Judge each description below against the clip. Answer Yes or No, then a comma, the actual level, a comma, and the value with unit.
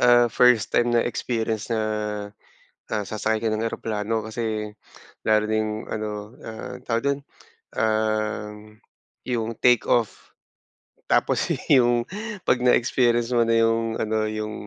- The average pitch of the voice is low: Yes, low, 110 Hz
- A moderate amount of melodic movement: No, narrow, 1.6 semitones